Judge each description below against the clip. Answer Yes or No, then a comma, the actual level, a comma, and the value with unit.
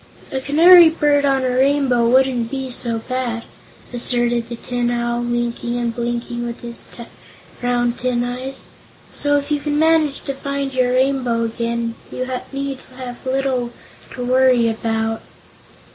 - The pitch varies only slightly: Yes, narrow, 2.2 semitones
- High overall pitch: Yes, very high, 250 Hz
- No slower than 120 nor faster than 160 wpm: Yes, average, 145 wpm